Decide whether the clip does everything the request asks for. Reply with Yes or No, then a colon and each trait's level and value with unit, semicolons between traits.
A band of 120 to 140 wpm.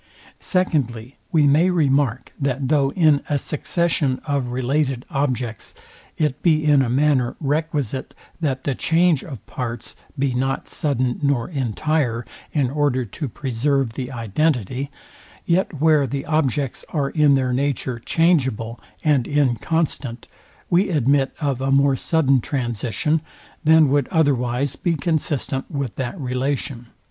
Yes: slow, 135 wpm